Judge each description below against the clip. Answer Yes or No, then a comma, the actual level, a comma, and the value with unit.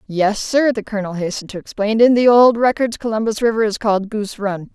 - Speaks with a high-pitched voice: Yes, high, 215 Hz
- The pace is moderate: No, fast, 215 wpm